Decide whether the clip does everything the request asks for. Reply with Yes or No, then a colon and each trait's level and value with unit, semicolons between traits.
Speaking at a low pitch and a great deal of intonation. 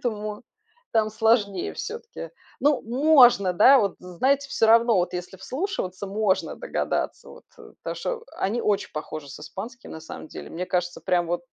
No: high, 215 Hz; wide, 6.0 semitones